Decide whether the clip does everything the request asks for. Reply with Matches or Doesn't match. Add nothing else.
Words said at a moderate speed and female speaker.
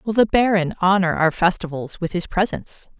Matches